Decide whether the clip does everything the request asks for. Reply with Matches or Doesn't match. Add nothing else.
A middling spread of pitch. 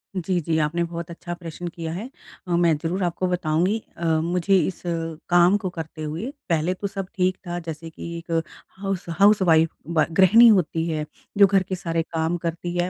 Doesn't match